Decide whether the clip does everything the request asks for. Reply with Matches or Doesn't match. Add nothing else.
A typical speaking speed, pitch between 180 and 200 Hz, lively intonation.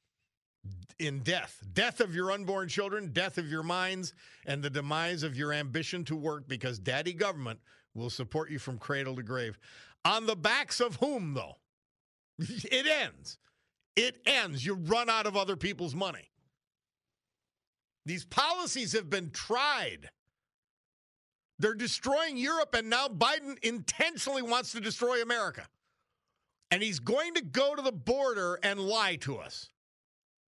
Matches